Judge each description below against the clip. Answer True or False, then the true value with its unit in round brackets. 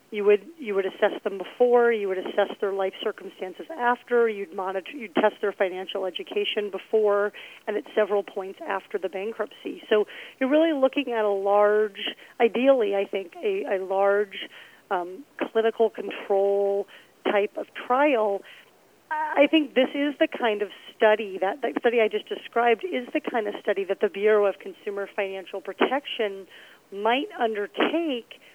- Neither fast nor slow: True (160 wpm)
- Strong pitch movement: False (3.6 semitones)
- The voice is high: True (210 Hz)